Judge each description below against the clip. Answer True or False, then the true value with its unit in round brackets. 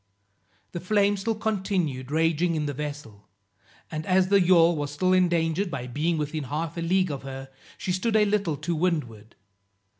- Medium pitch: True (165 Hz)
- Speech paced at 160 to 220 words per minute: True (175 wpm)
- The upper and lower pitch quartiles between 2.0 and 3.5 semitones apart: False (4.1 semitones)